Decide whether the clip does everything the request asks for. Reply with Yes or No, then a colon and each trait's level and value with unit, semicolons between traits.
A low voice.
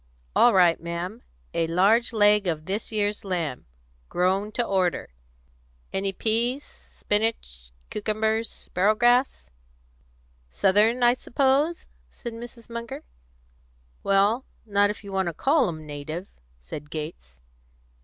No: high, 205 Hz